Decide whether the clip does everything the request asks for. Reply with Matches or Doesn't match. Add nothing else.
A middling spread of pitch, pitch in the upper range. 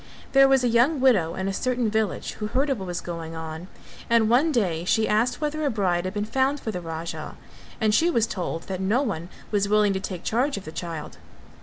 Doesn't match